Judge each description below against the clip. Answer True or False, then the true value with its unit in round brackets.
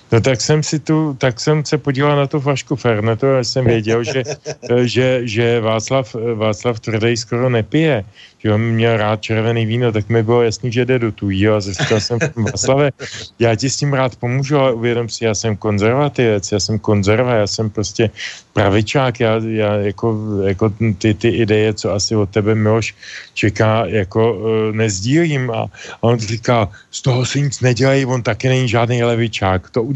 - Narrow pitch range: False (3.0 semitones)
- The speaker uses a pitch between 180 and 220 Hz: False (115 Hz)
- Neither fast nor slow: False (180 wpm)